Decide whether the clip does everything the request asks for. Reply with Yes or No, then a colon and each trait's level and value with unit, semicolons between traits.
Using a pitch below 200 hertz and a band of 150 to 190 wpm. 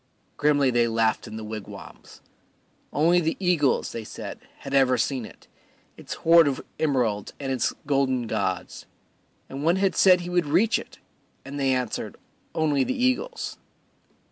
Yes: medium, 140 Hz; average, 155 wpm